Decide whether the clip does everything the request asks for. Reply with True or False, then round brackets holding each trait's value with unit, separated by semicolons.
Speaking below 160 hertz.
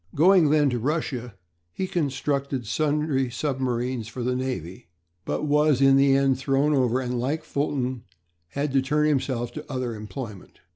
True (135 Hz)